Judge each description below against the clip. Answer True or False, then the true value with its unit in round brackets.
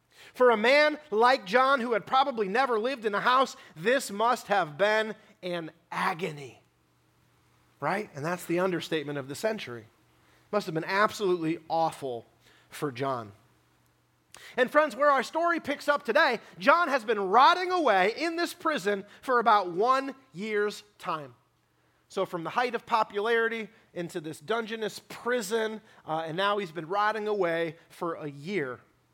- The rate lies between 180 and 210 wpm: False (155 wpm)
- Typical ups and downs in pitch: False (7.0 semitones)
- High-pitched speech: True (205 Hz)